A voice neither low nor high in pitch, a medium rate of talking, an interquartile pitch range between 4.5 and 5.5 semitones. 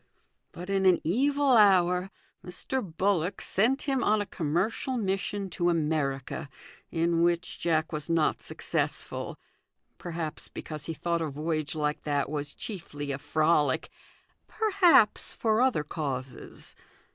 No: medium, 170 Hz; slow, 130 wpm; average, 4.9 semitones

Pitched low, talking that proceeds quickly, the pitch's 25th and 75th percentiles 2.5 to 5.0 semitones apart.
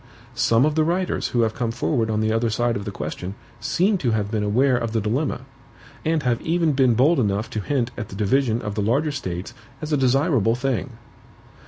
Yes: low, 120 Hz; fast, 215 wpm; average, 4.4 semitones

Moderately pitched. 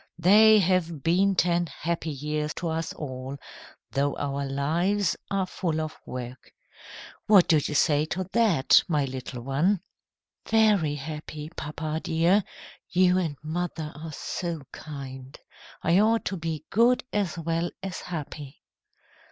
Yes: medium, 160 Hz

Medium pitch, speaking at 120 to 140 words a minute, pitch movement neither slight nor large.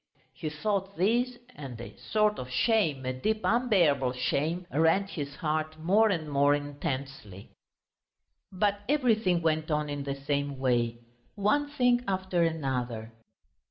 No: medium, 155 Hz; slow, 135 wpm; wide, 6.6 semitones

